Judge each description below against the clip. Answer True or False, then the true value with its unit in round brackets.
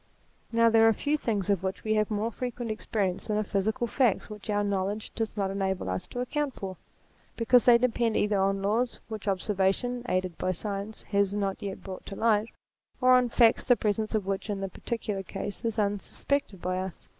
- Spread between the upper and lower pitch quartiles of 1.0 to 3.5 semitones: True (2.9 semitones)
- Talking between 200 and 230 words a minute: True (205 wpm)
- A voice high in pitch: True (210 Hz)